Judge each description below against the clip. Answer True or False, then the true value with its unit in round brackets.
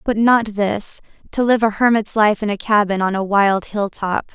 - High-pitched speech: True (210 Hz)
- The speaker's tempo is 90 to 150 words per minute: False (205 wpm)